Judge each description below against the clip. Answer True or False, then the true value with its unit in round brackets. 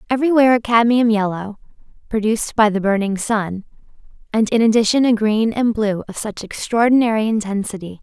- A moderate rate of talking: True (150 wpm)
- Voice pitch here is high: True (220 Hz)